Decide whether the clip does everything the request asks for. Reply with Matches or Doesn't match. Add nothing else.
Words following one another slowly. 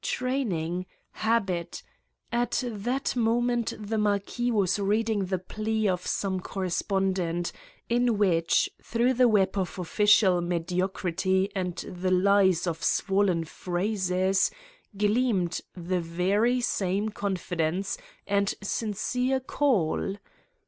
Matches